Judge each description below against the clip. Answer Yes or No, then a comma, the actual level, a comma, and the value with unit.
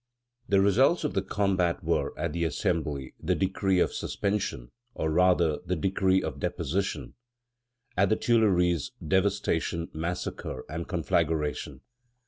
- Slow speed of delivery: Yes, slow, 125 wpm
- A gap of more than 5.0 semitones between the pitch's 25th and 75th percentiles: No, average, 3.5 semitones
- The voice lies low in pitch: Yes, very low, 90 Hz